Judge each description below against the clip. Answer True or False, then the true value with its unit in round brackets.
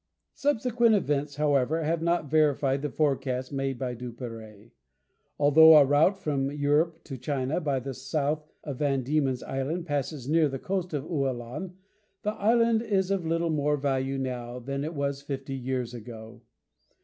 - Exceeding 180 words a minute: False (160 wpm)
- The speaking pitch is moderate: True (145 Hz)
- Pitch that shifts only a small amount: False (3.4 semitones)